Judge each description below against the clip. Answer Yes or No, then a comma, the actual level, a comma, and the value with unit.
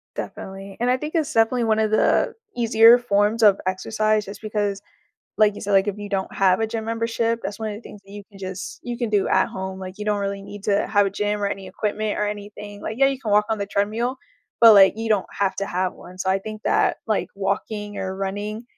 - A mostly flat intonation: Yes, narrow, 2.0 semitones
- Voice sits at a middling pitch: No, high, 210 Hz